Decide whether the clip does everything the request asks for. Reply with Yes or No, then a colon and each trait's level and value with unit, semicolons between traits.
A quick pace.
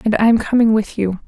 Yes: fast, 235 wpm